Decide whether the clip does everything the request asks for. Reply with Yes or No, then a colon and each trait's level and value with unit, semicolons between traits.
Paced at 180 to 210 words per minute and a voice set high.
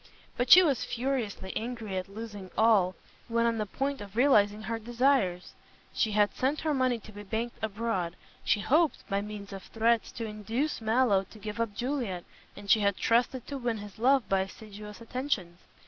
Yes: average, 185 wpm; high, 220 Hz